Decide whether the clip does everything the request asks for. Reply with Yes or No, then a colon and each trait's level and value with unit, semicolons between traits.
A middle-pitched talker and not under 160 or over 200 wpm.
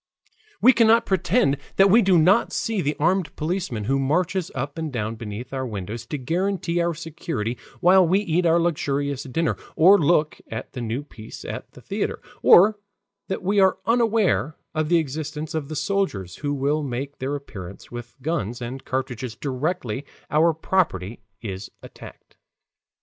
Yes: medium, 150 Hz; average, 165 wpm